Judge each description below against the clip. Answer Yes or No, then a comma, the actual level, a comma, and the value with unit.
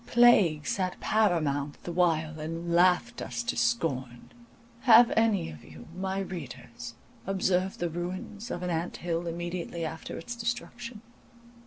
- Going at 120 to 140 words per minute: Yes, slow, 135 wpm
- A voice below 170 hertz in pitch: No, medium, 175 Hz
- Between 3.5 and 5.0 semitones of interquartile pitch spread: Yes, average, 4.0 semitones